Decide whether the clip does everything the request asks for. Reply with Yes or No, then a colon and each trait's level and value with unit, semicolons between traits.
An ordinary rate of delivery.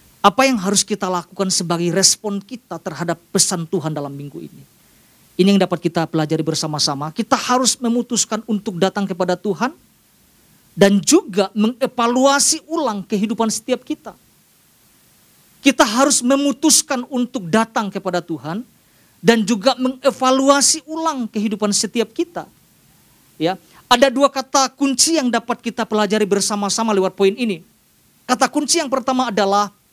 Yes: average, 130 wpm